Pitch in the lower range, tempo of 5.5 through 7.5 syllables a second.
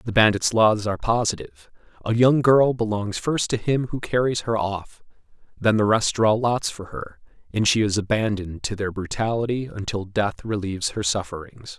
No: low, 105 Hz; 5.1 syllables/s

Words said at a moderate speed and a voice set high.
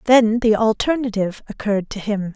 Yes: average, 155 wpm; high, 215 Hz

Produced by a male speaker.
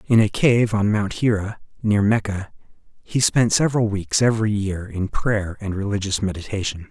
Yes: male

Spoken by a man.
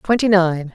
No: female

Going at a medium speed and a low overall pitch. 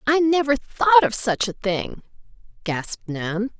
No: average, 150 wpm; high, 235 Hz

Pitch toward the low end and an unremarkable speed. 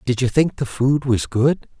No: low, 125 Hz; fast, 235 wpm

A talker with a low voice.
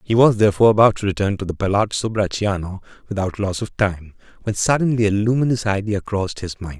Yes: low, 105 Hz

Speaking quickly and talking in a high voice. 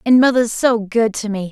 Yes: fast, 235 wpm; high, 225 Hz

